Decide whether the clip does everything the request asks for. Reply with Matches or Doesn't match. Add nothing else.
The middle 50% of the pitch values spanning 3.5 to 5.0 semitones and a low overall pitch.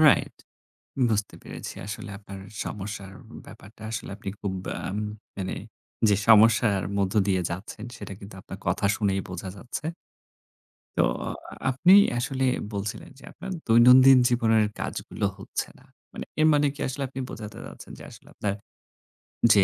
Matches